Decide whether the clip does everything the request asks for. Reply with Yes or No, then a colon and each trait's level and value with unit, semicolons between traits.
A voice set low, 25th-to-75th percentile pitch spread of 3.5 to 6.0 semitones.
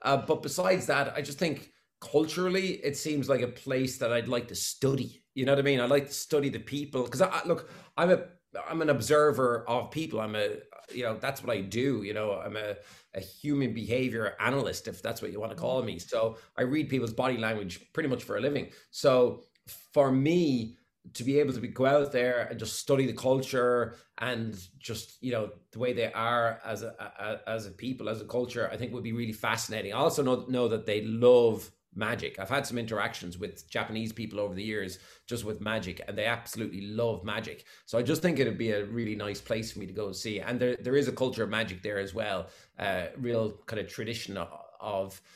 Yes: low, 120 Hz; average, 3.8 semitones